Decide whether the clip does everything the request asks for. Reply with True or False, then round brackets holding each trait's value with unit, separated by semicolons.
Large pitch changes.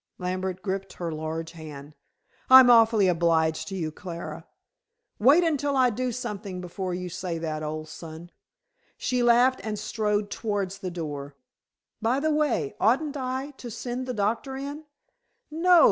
True (7.0 semitones)